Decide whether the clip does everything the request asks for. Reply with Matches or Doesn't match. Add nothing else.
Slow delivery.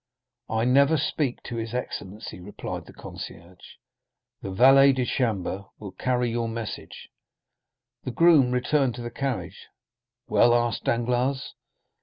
Matches